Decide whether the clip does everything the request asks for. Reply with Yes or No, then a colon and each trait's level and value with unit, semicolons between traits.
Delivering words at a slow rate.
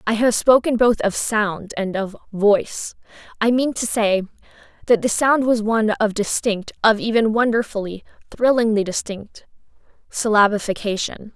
Yes: slow, 125 wpm